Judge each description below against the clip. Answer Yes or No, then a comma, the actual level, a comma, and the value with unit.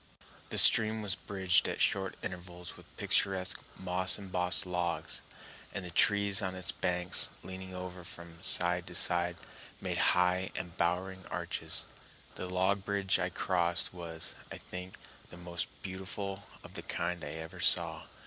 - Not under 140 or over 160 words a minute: Yes, average, 150 wpm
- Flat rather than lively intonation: Yes, narrow, 1.3 semitones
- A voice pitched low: Yes, very low, 90 Hz